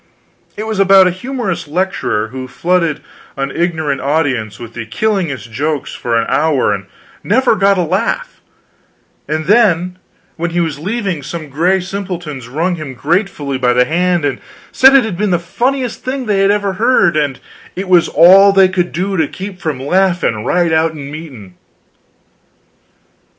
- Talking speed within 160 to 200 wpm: Yes, average, 165 wpm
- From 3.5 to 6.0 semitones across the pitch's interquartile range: Yes, average, 5.1 semitones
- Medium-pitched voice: Yes, medium, 175 Hz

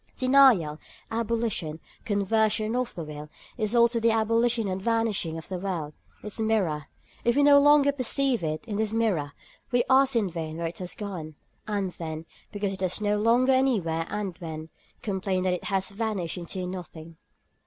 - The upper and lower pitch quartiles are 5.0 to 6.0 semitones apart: Yes, average, 5.3 semitones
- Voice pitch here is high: Yes, high, 205 Hz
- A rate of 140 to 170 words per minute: No, average, 180 wpm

